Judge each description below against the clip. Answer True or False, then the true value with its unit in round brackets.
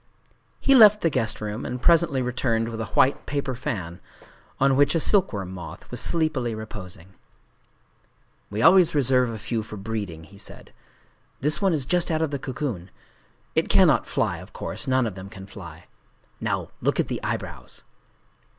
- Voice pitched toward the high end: False (125 Hz)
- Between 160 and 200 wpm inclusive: True (170 wpm)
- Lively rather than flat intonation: True (6.0 semitones)